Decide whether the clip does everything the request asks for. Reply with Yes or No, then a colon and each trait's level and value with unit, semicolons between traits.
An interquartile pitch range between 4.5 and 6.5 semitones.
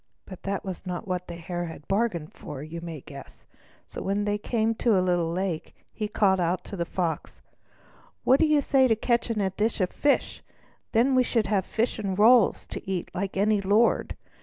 No: average, 4.1 semitones